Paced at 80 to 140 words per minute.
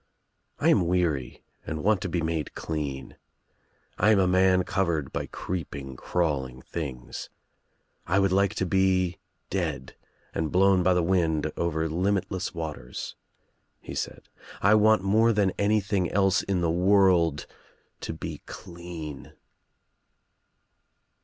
Yes: slow, 135 wpm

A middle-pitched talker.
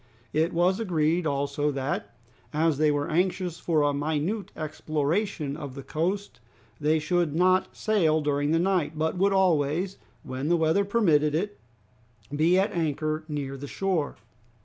Yes: medium, 160 Hz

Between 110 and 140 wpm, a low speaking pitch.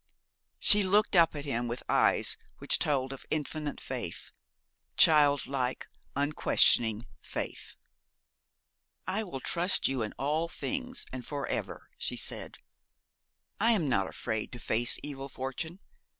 No: slow, 135 wpm; medium, 145 Hz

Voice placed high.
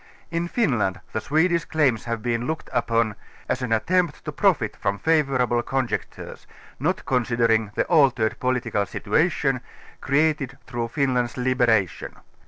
No: low, 125 Hz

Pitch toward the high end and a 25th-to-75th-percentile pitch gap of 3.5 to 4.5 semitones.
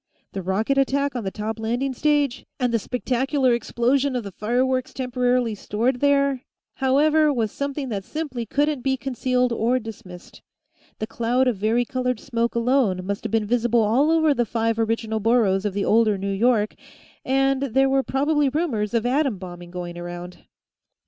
Yes: high, 245 Hz; average, 3.8 semitones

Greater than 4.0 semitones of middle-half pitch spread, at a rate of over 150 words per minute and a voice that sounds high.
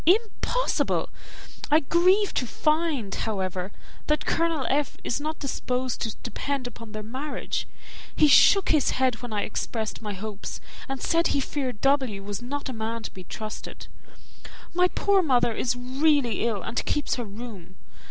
Yes: wide, 5.6 semitones; average, 160 wpm; very high, 255 Hz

